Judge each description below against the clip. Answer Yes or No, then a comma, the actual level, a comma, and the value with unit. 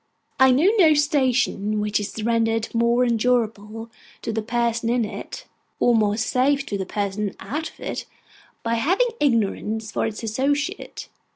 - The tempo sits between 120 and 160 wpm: Yes, average, 155 wpm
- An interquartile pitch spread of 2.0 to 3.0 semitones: No, average, 3.4 semitones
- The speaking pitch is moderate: No, high, 230 Hz